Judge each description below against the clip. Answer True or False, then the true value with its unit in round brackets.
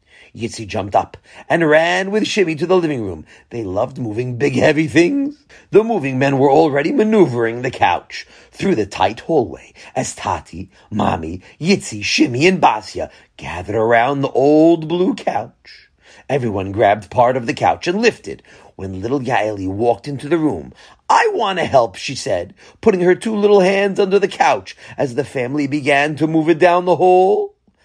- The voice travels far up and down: True (7.7 semitones)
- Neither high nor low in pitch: True (145 Hz)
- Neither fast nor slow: True (170 wpm)